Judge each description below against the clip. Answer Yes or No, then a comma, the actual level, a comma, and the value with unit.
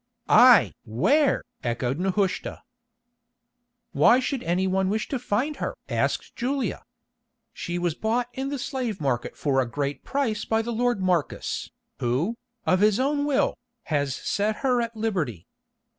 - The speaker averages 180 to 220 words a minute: No, average, 145 wpm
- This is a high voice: Yes, high, 210 Hz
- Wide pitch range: Yes, wide, 7.5 semitones